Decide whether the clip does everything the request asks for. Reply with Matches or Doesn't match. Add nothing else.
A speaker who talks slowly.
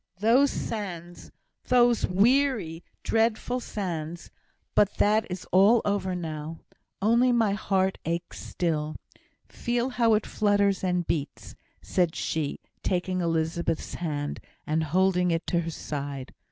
Matches